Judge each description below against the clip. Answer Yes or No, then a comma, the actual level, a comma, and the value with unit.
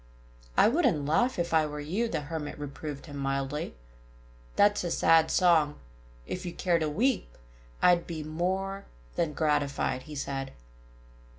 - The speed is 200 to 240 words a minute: No, average, 150 wpm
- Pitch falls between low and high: Yes, medium, 160 Hz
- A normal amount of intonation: Yes, average, 3.6 semitones